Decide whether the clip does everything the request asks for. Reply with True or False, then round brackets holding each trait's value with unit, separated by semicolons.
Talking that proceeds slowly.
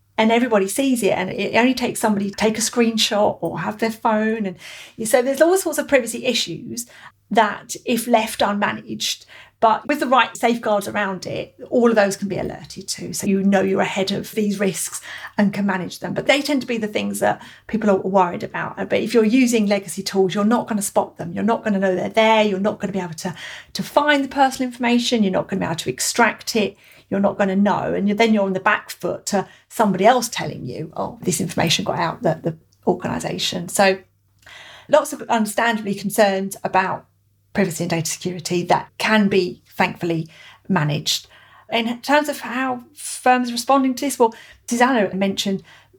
False (205 wpm)